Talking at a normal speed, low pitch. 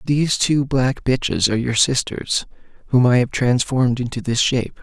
Yes: average, 175 wpm; low, 125 Hz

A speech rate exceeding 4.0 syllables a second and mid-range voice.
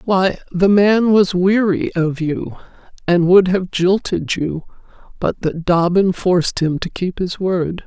No: 3.8 syllables/s; medium, 180 Hz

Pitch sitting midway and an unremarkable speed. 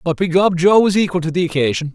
No: medium, 175 Hz; fast, 245 wpm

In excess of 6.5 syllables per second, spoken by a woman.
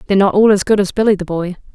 Yes: 7.8 syllables/s; female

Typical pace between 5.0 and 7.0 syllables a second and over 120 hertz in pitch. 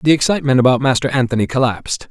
No: 7.5 syllables/s; low, 130 Hz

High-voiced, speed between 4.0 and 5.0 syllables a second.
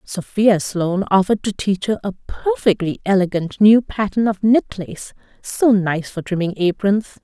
Yes: high, 200 Hz; 4.6 syllables/s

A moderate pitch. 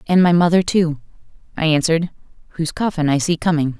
Yes: medium, 165 Hz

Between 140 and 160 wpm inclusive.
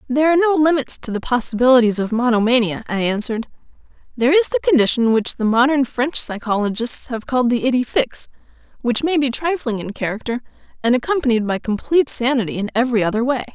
No: average, 175 wpm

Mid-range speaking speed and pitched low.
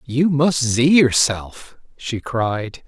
No: slow, 125 wpm; low, 130 Hz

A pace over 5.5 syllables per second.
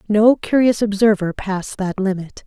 No: 4.8 syllables/s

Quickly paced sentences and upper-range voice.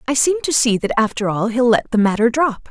Yes: fast, 265 wpm; high, 235 Hz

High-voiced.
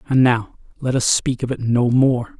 No: low, 125 Hz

